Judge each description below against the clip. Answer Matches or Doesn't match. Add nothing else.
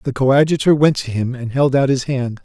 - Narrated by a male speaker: Matches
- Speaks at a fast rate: Matches